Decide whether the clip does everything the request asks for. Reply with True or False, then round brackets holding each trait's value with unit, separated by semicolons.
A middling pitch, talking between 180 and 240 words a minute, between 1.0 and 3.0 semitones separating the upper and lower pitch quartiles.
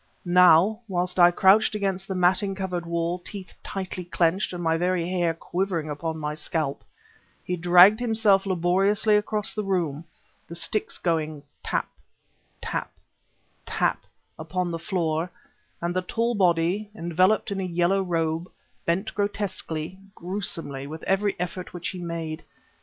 False (180 Hz; 140 wpm; 2.6 semitones)